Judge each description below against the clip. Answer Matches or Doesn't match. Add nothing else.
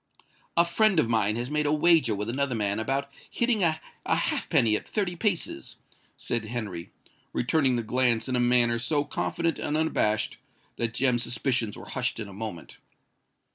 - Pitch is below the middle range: Matches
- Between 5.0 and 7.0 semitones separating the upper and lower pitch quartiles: Matches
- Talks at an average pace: Matches